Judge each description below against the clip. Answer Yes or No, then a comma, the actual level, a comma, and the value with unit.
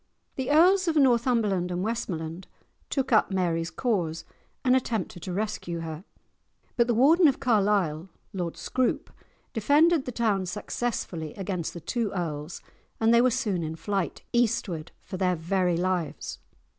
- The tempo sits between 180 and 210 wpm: No, average, 145 wpm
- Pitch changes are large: Yes, wide, 5.7 semitones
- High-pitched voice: Yes, high, 200 Hz